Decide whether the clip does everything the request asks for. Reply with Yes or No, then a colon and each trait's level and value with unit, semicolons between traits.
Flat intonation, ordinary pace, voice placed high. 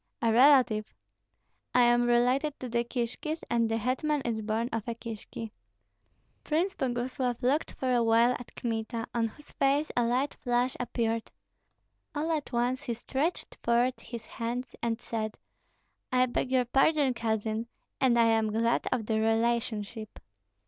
Yes: narrow, 2.2 semitones; average, 155 wpm; high, 240 Hz